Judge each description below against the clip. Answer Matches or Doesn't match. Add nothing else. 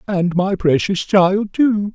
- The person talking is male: Matches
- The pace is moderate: Matches